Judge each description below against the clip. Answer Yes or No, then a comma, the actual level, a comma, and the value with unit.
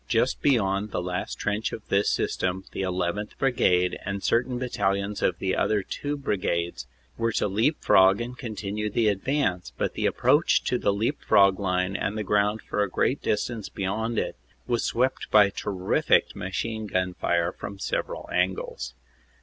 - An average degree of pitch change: Yes, average, 3.4 semitones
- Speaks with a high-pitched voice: No, low, 100 Hz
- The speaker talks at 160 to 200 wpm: Yes, average, 175 wpm